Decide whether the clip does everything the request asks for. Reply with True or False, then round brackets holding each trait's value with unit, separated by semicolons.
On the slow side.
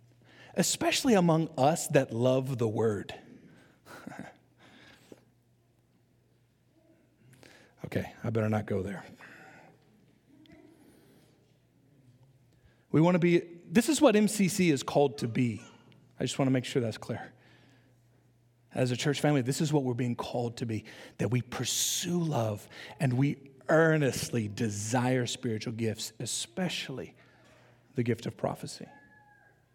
True (120 wpm)